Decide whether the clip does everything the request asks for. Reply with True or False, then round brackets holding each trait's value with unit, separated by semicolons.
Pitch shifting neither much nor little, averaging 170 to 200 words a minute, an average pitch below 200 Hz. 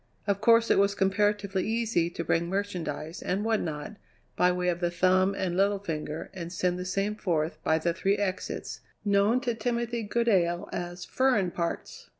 True (3.1 semitones; 175 wpm; 190 Hz)